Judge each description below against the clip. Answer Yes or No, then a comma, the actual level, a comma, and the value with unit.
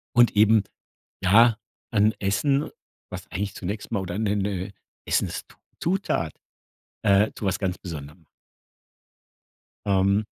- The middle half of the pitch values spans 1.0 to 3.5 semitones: Yes, narrow, 2.4 semitones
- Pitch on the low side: Yes, low, 100 Hz